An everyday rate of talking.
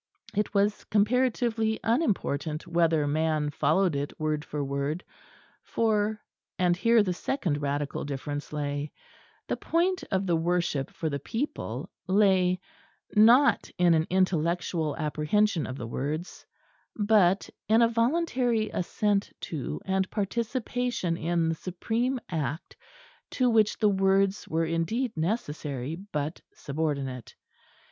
No: slow, 125 wpm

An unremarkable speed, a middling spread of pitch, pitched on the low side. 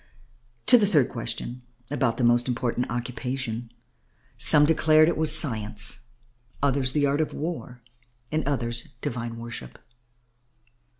No: slow, 125 wpm; average, 3.9 semitones; low, 125 Hz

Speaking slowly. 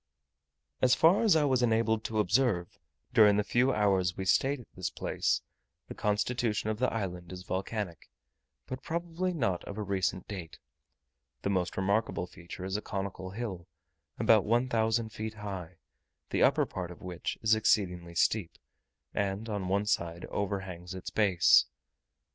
No: average, 160 wpm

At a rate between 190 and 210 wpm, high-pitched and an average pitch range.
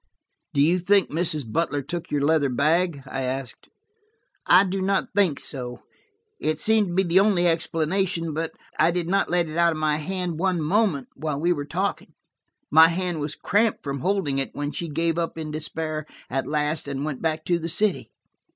No: average, 195 wpm; medium, 160 Hz; average, 3.3 semitones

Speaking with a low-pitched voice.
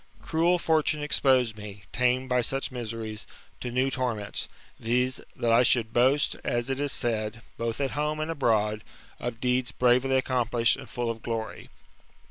Yes: low, 125 Hz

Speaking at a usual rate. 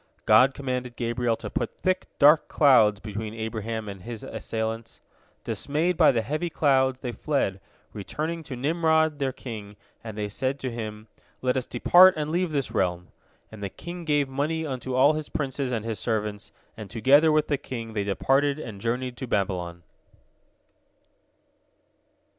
Yes: average, 160 wpm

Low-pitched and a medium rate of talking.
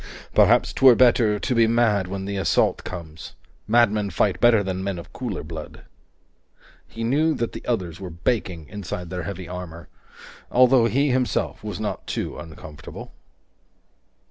Yes: low, 100 Hz; average, 150 wpm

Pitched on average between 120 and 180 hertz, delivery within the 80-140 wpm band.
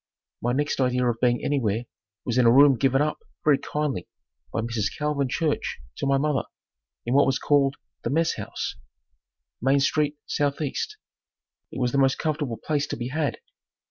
No: low, 135 Hz; average, 175 wpm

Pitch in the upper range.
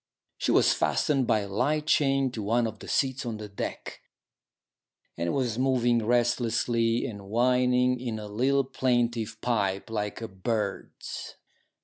No: low, 120 Hz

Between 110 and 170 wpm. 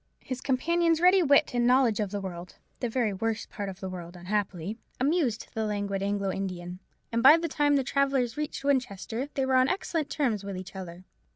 No: average, 190 wpm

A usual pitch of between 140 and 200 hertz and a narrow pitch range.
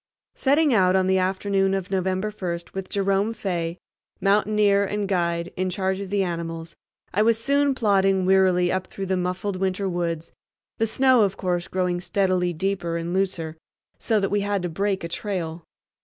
Yes: high, 190 Hz; narrow, 2.2 semitones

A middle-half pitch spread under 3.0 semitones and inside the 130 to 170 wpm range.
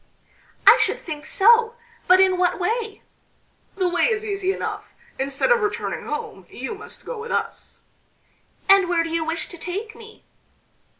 No: average, 4.8 semitones; average, 165 wpm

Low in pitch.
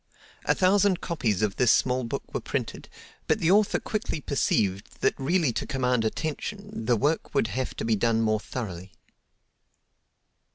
Yes: low, 125 Hz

